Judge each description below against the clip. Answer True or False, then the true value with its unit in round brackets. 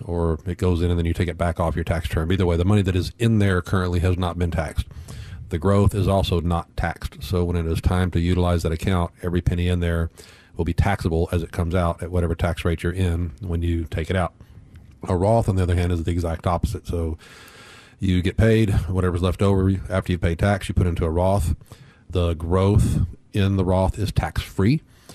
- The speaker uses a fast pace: True (235 wpm)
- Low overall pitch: True (90 Hz)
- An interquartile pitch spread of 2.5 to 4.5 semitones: False (2.1 semitones)